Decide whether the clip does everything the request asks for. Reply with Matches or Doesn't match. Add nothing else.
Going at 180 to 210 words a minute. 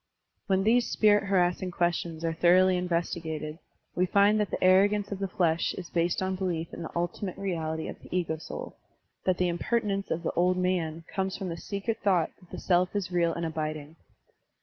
Matches